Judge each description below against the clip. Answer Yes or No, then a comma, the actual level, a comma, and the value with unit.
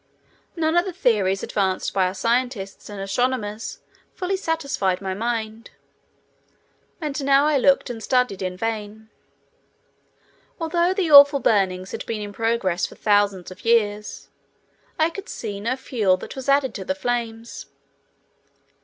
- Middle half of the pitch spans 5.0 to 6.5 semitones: Yes, wide, 5.6 semitones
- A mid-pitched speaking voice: No, high, 225 Hz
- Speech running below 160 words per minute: Yes, average, 145 wpm